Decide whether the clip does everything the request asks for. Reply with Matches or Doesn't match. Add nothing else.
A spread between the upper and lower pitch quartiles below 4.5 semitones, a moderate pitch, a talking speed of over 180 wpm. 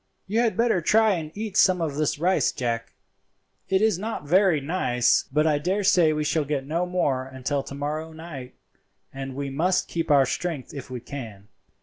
Doesn't match